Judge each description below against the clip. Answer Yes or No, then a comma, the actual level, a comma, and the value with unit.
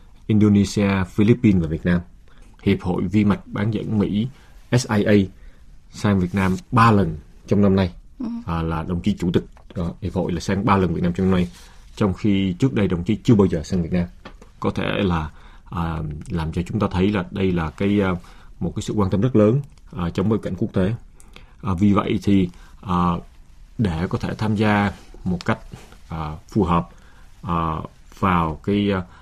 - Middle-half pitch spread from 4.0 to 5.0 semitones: No, average, 3.5 semitones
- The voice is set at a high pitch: No, very low, 95 Hz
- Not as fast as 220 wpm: Yes, average, 195 wpm